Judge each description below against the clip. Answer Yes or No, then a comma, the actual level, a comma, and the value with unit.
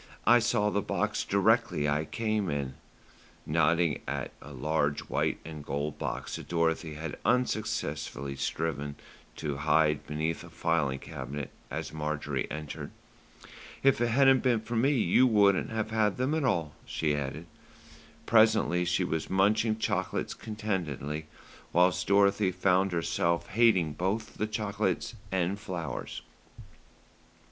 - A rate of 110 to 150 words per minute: Yes, slow, 135 wpm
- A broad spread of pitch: Yes, wide, 6.1 semitones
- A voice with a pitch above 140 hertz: No, very low, 85 Hz